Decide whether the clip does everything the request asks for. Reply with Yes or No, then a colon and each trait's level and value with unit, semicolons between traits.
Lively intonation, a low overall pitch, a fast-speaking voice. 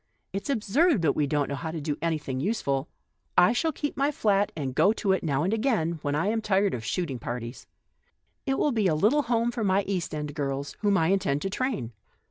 No: wide, 7.2 semitones; high, 190 Hz; fast, 240 wpm